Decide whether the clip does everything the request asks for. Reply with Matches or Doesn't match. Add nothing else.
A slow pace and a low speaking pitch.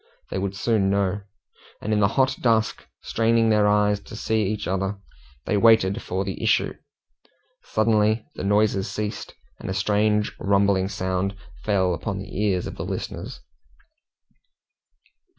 Doesn't match